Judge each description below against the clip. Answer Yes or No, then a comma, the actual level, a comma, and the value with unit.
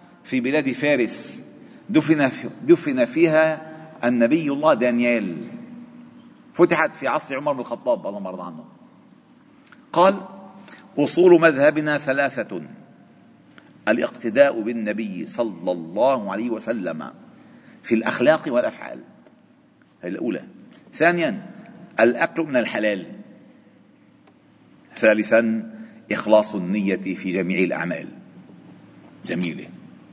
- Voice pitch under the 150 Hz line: No, medium, 165 Hz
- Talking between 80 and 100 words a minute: Yes, average, 85 wpm